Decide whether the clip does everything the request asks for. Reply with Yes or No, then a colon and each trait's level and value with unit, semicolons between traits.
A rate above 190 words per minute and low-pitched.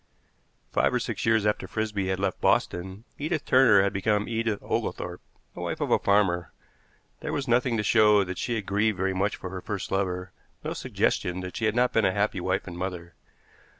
Yes: fast, 205 wpm; low, 100 Hz